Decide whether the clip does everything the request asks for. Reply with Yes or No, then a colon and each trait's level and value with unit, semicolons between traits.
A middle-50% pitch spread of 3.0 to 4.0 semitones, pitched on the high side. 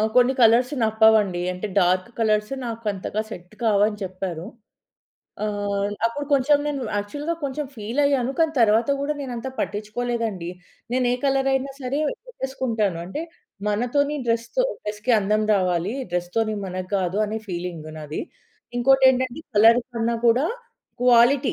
No: average, 4.4 semitones; high, 225 Hz